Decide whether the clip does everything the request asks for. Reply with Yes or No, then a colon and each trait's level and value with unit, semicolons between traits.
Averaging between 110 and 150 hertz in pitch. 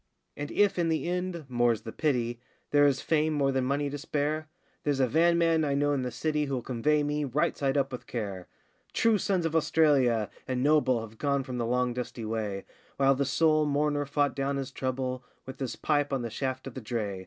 Yes: medium, 140 Hz